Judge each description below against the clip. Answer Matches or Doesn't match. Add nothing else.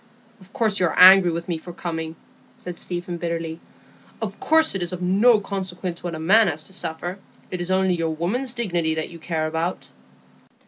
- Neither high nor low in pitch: Matches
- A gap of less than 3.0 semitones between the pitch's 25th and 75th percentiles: Matches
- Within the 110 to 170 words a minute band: Doesn't match